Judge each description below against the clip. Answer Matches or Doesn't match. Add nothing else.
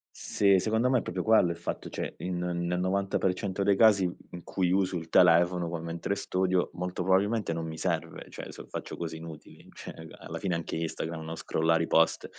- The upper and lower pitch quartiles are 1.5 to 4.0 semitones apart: Matches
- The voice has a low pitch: Matches